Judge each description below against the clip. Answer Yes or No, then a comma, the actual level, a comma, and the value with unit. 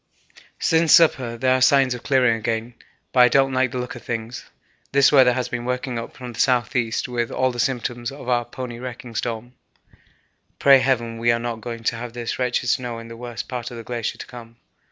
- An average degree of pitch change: No, narrow, 1.6 semitones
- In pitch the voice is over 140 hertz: No, low, 120 Hz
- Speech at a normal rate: No, fast, 215 wpm